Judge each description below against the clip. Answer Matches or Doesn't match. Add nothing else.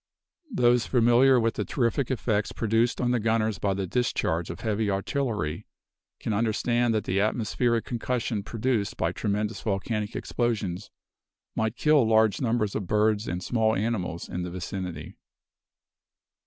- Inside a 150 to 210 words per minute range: Doesn't match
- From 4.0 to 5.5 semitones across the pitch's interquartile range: Doesn't match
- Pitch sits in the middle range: Doesn't match